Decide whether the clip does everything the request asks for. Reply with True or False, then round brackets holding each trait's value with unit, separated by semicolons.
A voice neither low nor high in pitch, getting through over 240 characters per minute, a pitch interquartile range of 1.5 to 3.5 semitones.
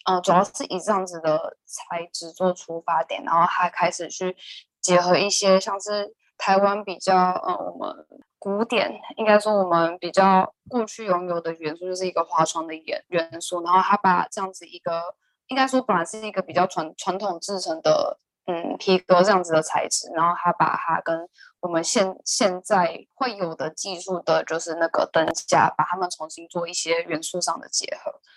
True (180 Hz; 280 characters per minute; 2.7 semitones)